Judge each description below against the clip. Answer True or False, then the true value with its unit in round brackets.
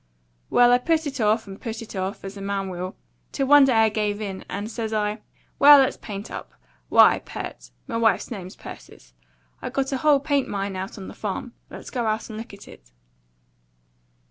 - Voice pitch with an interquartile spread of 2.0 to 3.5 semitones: False (4.0 semitones)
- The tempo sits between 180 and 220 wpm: True (200 wpm)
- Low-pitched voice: False (220 Hz)